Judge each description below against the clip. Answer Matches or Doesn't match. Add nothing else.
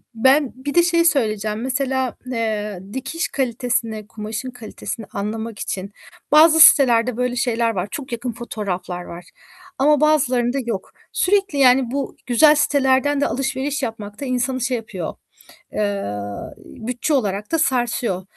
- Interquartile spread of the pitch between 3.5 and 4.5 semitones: Matches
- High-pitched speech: Matches